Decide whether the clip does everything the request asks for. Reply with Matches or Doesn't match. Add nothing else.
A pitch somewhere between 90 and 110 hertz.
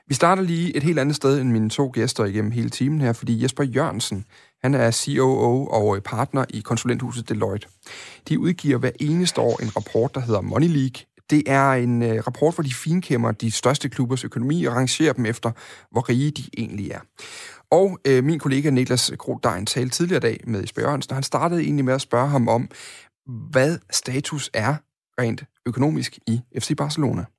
Doesn't match